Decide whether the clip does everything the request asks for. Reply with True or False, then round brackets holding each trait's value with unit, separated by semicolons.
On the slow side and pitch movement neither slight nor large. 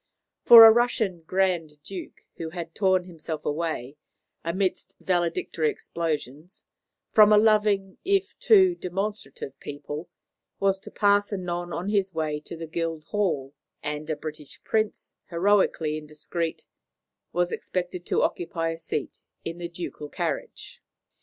True (130 wpm; 3.9 semitones)